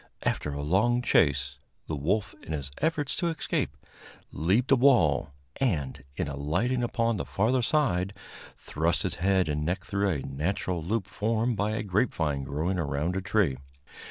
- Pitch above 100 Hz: No, very low, 95 Hz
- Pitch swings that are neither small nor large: No, wide, 7.4 semitones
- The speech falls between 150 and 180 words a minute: Yes, average, 160 wpm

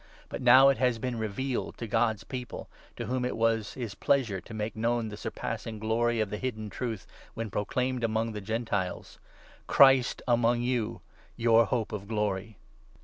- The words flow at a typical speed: Yes, average, 170 wpm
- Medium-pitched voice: No, low, 115 Hz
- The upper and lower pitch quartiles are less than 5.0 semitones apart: Yes, narrow, 2.4 semitones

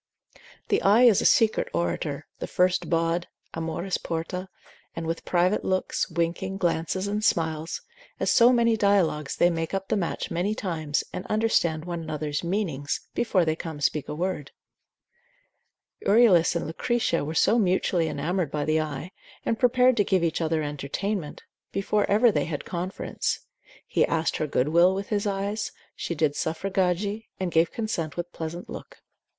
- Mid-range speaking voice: Yes, medium, 175 Hz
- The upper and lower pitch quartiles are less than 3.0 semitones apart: No, average, 3.8 semitones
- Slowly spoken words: No, average, 165 wpm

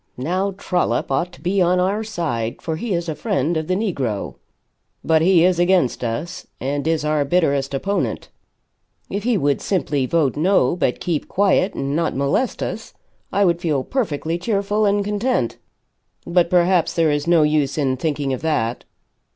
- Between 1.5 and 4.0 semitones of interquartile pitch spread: No, average, 4.7 semitones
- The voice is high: No, medium, 165 Hz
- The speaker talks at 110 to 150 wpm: No, average, 175 wpm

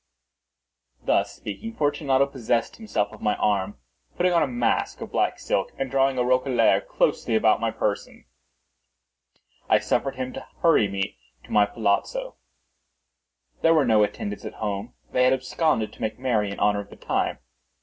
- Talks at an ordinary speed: Yes, average, 165 wpm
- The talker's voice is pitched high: No, low, 120 Hz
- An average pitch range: Yes, average, 4.7 semitones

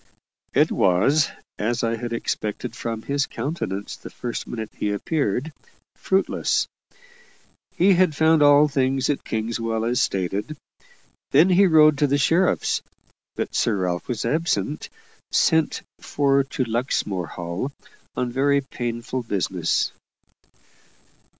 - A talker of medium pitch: No, low, 125 Hz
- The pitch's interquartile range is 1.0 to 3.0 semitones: No, average, 4.8 semitones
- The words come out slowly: Yes, slow, 125 wpm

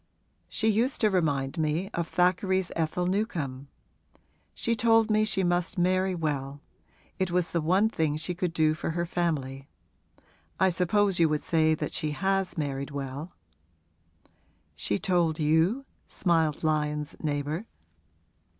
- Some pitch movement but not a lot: Yes, average, 3.8 semitones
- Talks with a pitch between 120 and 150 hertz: No, medium, 170 Hz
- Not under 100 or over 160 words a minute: Yes, average, 140 wpm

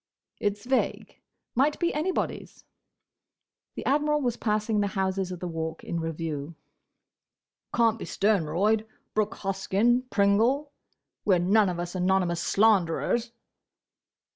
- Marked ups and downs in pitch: No, average, 4.6 semitones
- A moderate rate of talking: No, slow, 110 wpm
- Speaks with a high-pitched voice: Yes, high, 205 Hz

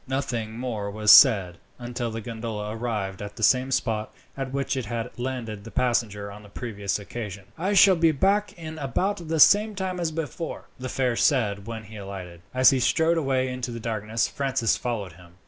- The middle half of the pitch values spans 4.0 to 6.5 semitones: Yes, average, 4.5 semitones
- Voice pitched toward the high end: No, low, 120 Hz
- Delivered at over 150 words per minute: Yes, average, 195 wpm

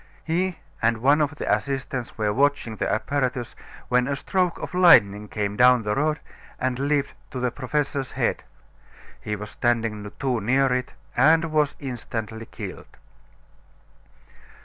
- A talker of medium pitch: No, low, 130 Hz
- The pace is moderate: Yes, average, 145 wpm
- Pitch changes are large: No, average, 4.1 semitones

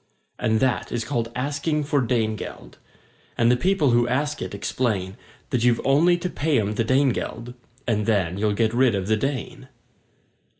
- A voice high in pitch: No, low, 120 Hz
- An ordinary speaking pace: Yes, average, 180 wpm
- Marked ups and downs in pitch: No, average, 4.2 semitones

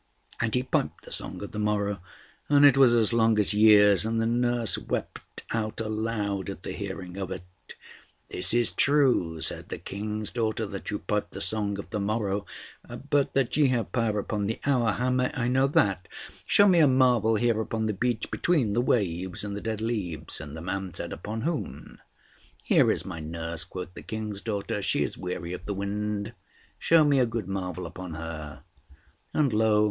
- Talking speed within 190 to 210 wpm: Yes, average, 195 wpm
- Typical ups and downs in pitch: Yes, average, 3.4 semitones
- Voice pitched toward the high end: No, low, 105 Hz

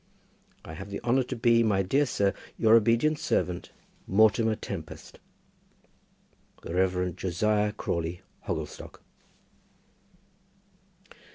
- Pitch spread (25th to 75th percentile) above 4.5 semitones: No, average, 4.1 semitones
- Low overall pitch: Yes, low, 105 Hz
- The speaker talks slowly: Yes, slow, 105 wpm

